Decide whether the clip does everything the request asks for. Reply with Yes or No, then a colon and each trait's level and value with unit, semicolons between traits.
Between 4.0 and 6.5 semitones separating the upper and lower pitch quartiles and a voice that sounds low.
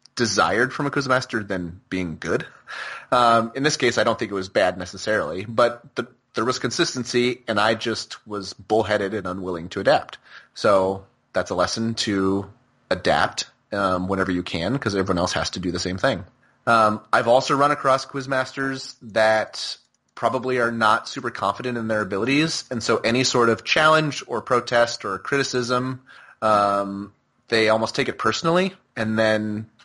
Yes: average, 4.4 semitones; low, 115 Hz